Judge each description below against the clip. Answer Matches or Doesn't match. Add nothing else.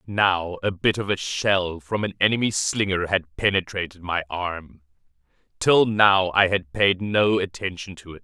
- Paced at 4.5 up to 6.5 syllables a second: Doesn't match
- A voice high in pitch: Doesn't match